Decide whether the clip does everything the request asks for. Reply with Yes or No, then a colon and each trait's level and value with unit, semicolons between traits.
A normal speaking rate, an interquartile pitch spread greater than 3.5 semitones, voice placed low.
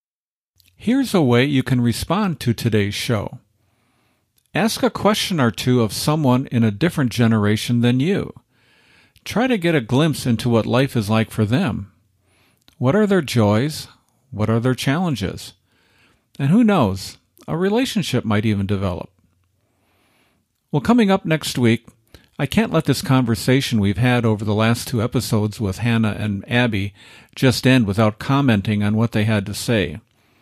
Yes: average, 160 wpm; average, 4.3 semitones; low, 120 Hz